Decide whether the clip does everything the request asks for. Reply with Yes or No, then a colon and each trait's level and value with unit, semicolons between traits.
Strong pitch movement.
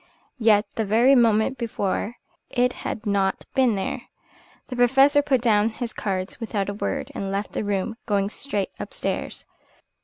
No: average, 3.4 semitones